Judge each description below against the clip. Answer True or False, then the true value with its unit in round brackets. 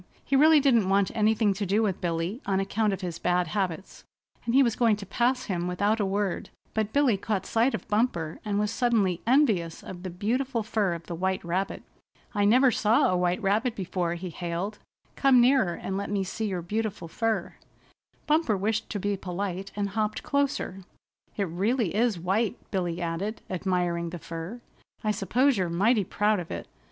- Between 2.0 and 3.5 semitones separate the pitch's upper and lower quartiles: False (3.9 semitones)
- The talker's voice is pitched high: True (200 Hz)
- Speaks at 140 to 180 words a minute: False (190 wpm)